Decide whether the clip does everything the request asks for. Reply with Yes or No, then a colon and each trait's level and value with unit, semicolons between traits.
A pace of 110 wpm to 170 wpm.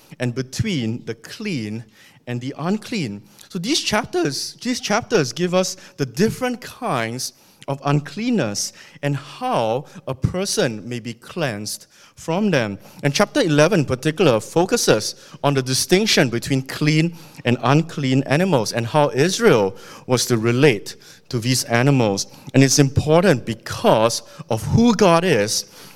Yes: average, 140 wpm